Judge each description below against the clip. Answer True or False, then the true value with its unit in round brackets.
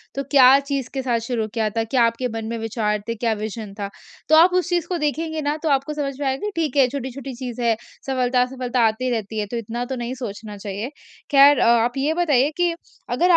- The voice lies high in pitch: True (255 Hz)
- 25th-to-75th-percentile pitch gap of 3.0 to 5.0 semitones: True (3.7 semitones)